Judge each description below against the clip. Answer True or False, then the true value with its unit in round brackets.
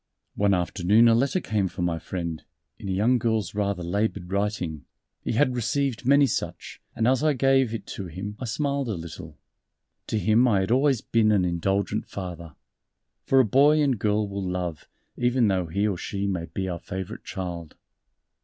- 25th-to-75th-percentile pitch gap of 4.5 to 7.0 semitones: True (5.0 semitones)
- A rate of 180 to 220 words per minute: True (185 wpm)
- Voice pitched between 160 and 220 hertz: False (105 Hz)